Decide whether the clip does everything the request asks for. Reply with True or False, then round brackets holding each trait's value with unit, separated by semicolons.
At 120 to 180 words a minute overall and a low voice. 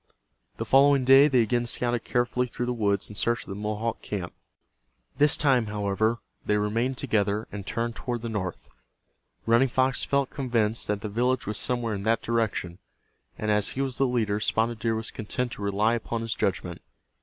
False (190 wpm; 115 Hz)